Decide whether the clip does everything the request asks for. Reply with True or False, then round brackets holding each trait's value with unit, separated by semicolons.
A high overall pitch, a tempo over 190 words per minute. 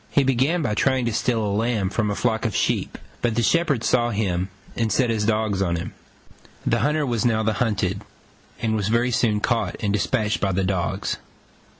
False (110 Hz; 205 wpm)